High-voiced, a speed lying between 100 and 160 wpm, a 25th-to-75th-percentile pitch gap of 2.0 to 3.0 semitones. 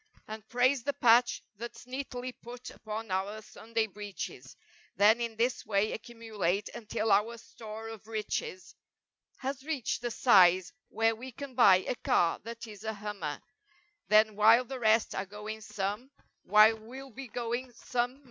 Yes: high, 225 Hz; average, 155 wpm; average, 2.7 semitones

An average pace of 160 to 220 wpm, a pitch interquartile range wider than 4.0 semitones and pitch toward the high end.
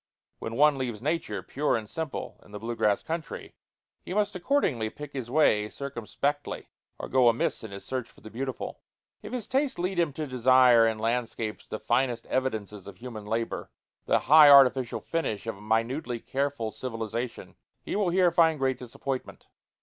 No: average, 175 wpm; average, 4.7 semitones; low, 130 Hz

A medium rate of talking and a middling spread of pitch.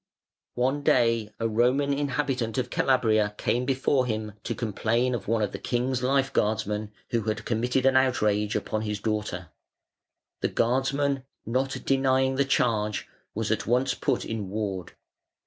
Yes: average, 150 wpm; average, 3.6 semitones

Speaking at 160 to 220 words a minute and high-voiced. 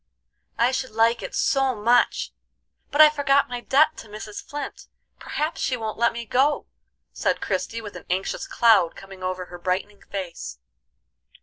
Yes: average, 165 wpm; high, 230 Hz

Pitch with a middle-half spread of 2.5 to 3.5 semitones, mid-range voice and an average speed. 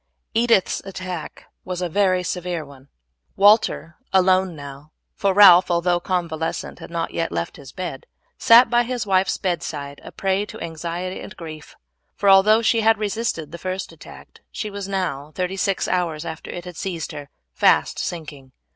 Yes: average, 3.2 semitones; medium, 180 Hz; average, 165 wpm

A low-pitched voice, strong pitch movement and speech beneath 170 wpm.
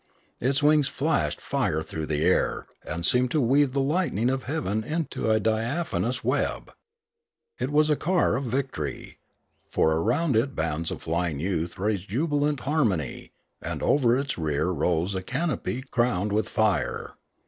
Yes: low, 120 Hz; wide, 8.1 semitones; average, 155 wpm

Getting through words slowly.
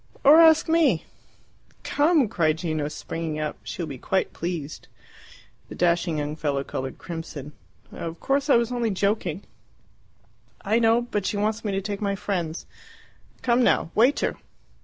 No: average, 155 wpm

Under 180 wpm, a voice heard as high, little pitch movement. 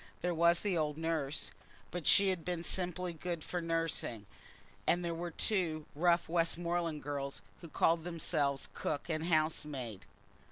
No: average, 150 wpm; medium, 165 Hz; narrow, 2.3 semitones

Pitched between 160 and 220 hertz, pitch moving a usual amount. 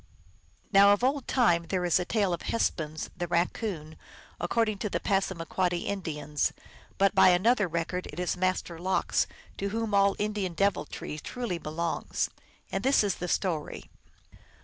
Yes: medium, 185 Hz; average, 3.1 semitones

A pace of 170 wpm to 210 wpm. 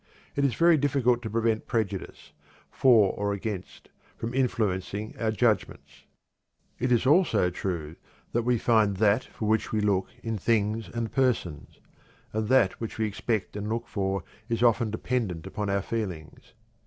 No: average, 155 wpm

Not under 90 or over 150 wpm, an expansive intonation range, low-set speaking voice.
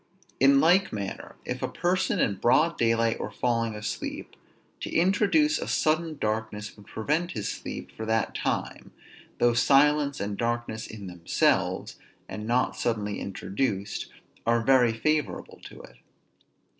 Yes: average, 140 wpm; wide, 5.8 semitones; low, 115 Hz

